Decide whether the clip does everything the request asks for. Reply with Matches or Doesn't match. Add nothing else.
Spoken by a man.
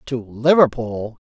Doesn't match